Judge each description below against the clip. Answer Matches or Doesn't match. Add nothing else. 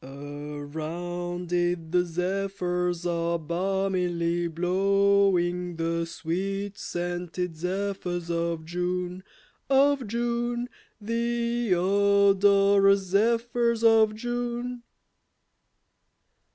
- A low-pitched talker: Doesn't match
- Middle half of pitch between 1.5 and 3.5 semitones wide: Matches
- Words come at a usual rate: Doesn't match